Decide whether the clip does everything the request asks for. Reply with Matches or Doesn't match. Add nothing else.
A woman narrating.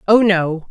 Matches